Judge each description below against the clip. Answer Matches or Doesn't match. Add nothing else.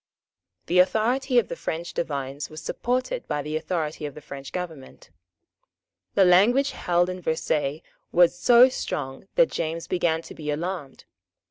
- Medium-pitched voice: Matches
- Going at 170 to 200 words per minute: Doesn't match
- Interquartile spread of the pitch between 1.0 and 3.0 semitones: Doesn't match